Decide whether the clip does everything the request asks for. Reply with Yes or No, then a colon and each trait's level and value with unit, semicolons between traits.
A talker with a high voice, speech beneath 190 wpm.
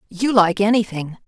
Yes: high, 200 Hz; average, 140 wpm